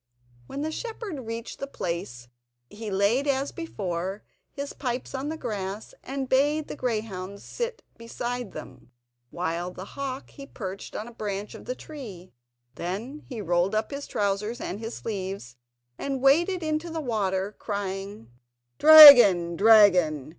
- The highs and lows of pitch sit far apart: Yes, wide, 6.4 semitones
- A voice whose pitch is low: No, high, 220 Hz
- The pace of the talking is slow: No, average, 145 wpm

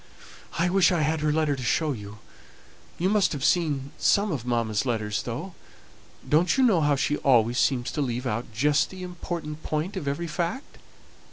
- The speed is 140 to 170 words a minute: No, average, 185 wpm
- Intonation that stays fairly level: No, wide, 5.5 semitones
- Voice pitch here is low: No, medium, 150 Hz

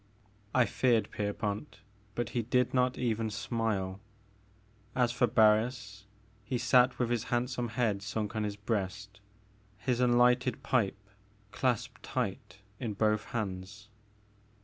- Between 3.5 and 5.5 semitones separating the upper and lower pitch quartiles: No, average, 3.1 semitones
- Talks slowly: Yes, slow, 125 wpm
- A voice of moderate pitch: No, low, 115 Hz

